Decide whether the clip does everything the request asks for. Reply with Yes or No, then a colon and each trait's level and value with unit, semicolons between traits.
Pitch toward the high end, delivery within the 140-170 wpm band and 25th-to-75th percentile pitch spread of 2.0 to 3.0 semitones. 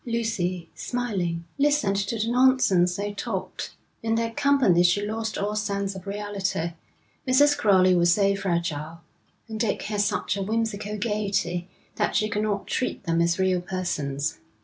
No: high, 200 Hz; average, 155 wpm; average, 3.7 semitones